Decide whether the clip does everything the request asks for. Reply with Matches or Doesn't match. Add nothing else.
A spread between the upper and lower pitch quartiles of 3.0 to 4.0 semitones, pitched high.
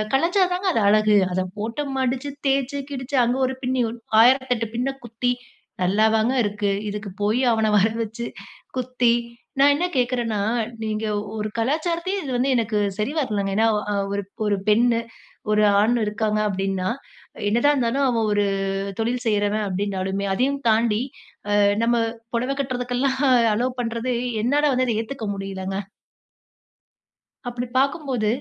Matches